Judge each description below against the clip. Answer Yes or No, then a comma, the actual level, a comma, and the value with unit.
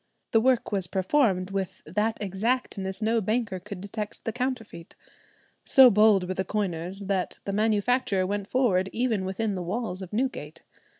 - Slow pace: No, average, 160 wpm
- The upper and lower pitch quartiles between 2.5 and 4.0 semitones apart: Yes, average, 3.1 semitones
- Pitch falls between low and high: No, high, 205 Hz